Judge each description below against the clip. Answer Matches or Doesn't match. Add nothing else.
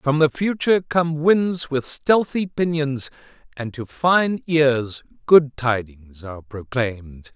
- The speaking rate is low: Matches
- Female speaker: Doesn't match